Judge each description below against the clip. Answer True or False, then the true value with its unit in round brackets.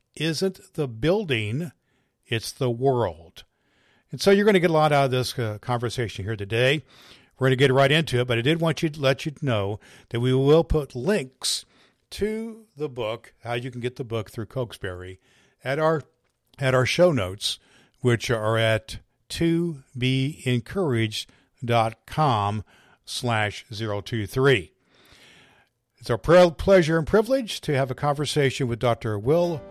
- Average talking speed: True (160 wpm)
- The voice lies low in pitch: True (130 Hz)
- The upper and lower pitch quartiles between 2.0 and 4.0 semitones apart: False (4.8 semitones)